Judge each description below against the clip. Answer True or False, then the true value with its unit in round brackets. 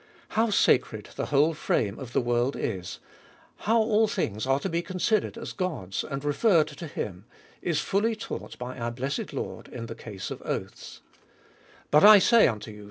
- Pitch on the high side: False (145 Hz)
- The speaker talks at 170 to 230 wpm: True (180 wpm)